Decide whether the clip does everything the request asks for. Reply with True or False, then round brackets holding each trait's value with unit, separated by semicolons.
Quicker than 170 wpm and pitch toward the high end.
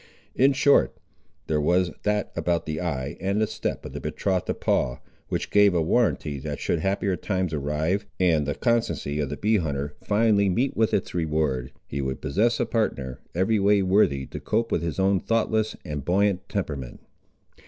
False (180 wpm; 90 Hz)